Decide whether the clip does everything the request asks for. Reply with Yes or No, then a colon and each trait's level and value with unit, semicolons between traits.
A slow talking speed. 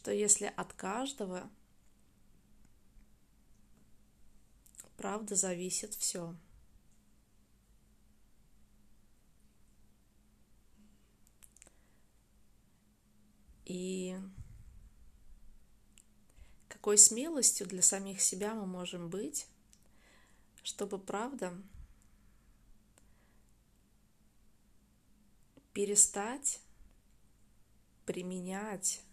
Yes: slow, 40 wpm